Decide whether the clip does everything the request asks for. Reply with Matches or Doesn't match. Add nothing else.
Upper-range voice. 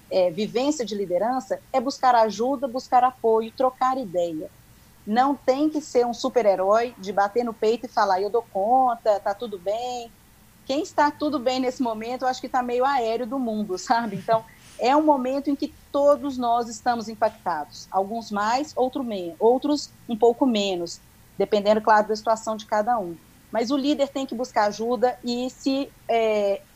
Matches